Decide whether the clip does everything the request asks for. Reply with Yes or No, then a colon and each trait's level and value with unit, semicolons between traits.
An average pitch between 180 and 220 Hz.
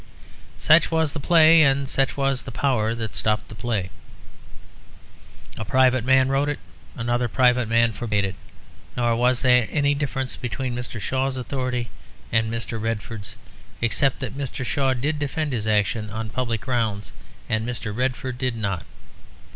No: low, 125 Hz